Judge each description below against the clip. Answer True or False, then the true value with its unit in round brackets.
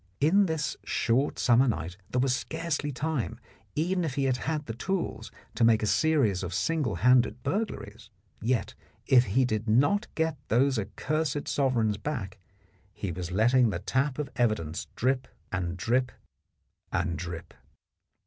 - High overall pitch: False (125 Hz)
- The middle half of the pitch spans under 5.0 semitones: False (5.6 semitones)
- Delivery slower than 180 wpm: True (150 wpm)